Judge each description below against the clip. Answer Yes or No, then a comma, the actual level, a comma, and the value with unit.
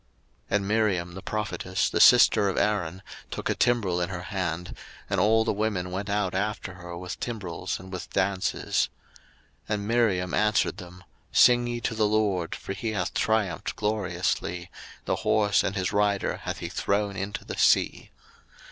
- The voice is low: Yes, low, 100 Hz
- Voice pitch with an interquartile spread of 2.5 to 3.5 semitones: Yes, average, 2.8 semitones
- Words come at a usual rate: Yes, average, 175 wpm